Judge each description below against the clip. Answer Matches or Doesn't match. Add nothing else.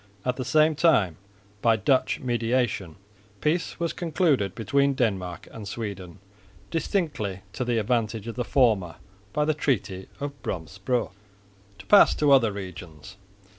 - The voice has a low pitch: Matches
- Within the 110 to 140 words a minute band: Matches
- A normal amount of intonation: Doesn't match